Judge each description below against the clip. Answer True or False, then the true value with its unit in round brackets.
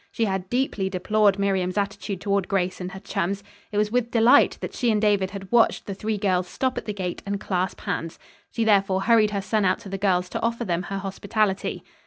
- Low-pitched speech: False (200 Hz)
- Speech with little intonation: True (2.1 semitones)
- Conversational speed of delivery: False (225 wpm)